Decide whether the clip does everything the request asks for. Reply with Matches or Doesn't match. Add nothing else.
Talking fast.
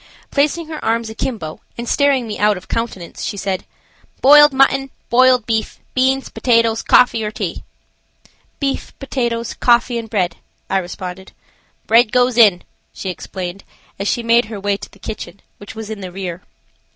Doesn't match